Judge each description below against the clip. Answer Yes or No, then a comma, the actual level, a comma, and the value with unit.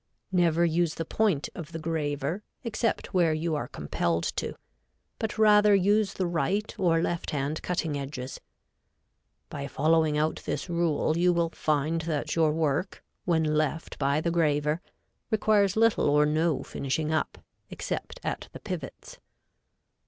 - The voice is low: No, medium, 160 Hz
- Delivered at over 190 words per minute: No, average, 145 wpm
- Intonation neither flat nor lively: Yes, average, 3.0 semitones